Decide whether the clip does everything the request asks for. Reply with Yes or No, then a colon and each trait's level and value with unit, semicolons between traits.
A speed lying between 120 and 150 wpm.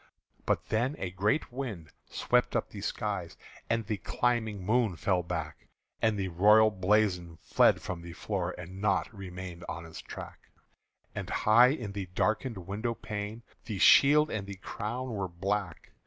No: average, 160 wpm